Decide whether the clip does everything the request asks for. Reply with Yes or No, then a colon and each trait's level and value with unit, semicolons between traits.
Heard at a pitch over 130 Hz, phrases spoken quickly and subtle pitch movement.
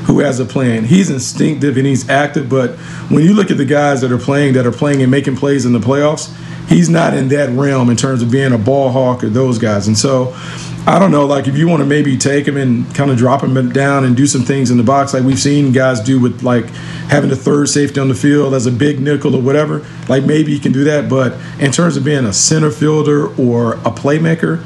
Yes: medium, 140 Hz; fast, 260 wpm; narrow, 2.2 semitones